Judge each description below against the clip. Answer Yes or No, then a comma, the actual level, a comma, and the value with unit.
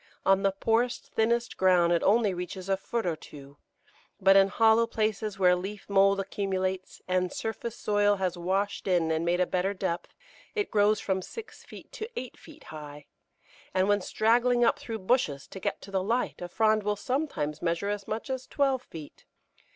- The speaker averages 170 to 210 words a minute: Yes, average, 185 wpm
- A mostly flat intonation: No, average, 3.6 semitones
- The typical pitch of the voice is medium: No, high, 195 Hz